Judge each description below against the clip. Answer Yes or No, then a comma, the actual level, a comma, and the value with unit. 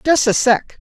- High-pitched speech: Yes, very high, 250 Hz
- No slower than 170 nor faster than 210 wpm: Yes, fast, 205 wpm